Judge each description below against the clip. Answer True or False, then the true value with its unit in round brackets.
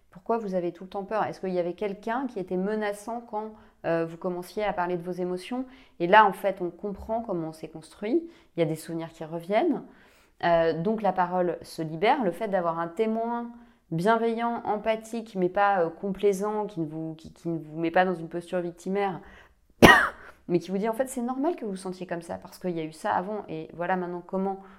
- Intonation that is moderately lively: True (3.9 semitones)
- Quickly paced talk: True (230 wpm)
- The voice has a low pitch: False (190 Hz)